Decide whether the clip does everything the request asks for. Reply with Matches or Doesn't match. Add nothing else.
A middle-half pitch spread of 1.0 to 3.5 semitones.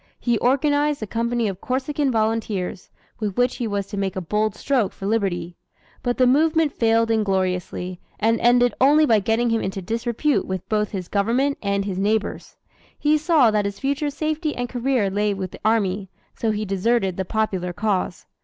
Doesn't match